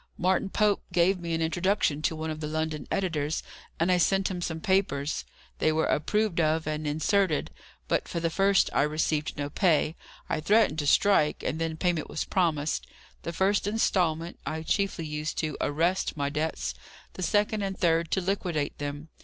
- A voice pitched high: No, medium, 165 Hz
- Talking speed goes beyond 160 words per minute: Yes, average, 180 wpm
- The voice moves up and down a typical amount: Yes, average, 3.5 semitones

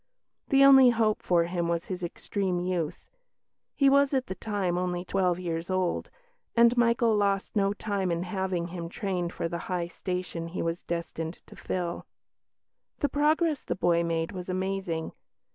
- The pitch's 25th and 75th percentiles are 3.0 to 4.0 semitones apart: Yes, average, 3.4 semitones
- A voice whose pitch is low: No, medium, 185 Hz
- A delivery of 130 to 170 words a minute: Yes, average, 165 wpm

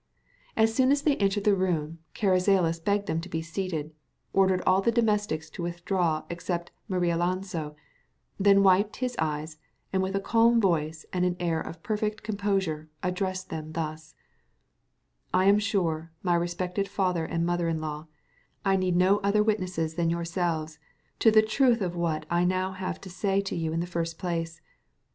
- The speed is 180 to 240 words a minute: No, average, 170 wpm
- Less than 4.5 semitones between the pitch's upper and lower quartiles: Yes, average, 3.2 semitones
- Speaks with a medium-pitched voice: Yes, medium, 180 Hz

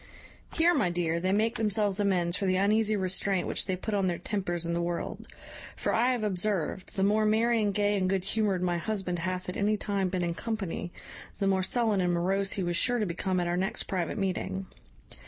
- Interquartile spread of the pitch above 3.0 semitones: No, average, 2.7 semitones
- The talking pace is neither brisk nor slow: No, fast, 220 wpm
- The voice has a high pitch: Yes, high, 195 Hz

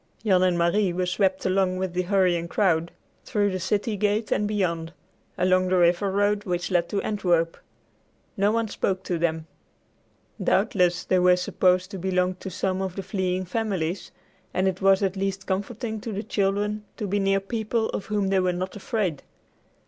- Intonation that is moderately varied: No, narrow, 2.0 semitones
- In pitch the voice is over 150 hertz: Yes, high, 190 Hz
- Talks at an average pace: Yes, average, 185 wpm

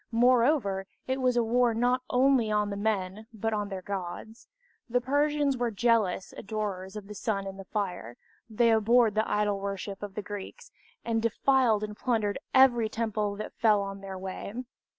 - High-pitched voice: Yes, high, 215 Hz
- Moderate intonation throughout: Yes, average, 3.2 semitones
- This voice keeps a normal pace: Yes, average, 175 wpm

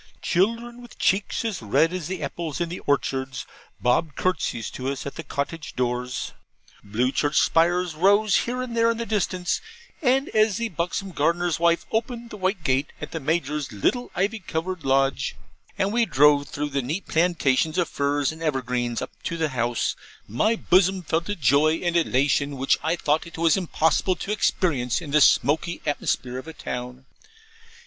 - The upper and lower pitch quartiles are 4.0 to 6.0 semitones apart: Yes, average, 5.2 semitones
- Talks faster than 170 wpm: Yes, average, 180 wpm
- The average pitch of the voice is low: No, medium, 165 Hz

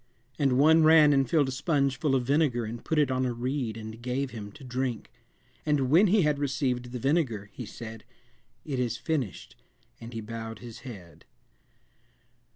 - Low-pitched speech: Yes, low, 130 Hz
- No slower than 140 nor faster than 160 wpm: No, average, 180 wpm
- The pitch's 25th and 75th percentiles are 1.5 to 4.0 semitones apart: Yes, average, 3.7 semitones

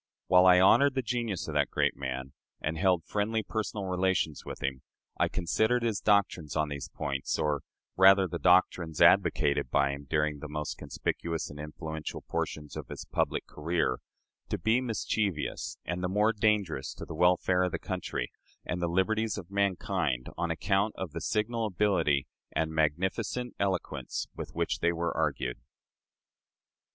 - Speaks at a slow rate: No, average, 165 wpm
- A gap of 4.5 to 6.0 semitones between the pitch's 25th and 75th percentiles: Yes, average, 4.9 semitones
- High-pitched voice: No, very low, 90 Hz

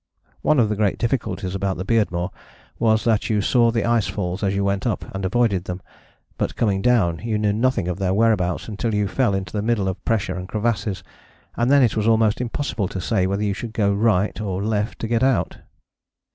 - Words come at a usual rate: No, fast, 215 wpm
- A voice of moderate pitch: No, low, 105 Hz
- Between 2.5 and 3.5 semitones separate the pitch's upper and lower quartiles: Yes, average, 3.0 semitones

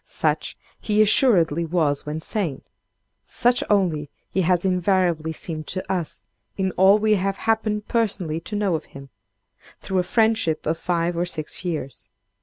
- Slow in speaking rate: No, average, 155 wpm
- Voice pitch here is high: No, medium, 180 Hz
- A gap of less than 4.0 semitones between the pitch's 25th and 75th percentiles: No, average, 4.3 semitones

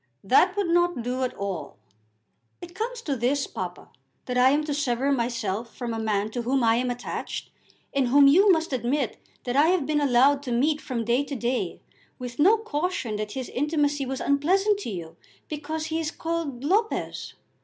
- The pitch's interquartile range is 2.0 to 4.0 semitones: No, average, 4.7 semitones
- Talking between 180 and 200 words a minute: Yes, average, 190 wpm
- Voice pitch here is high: Yes, very high, 275 Hz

